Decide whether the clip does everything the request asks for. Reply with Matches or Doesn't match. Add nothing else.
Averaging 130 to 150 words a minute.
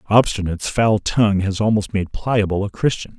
Doesn't match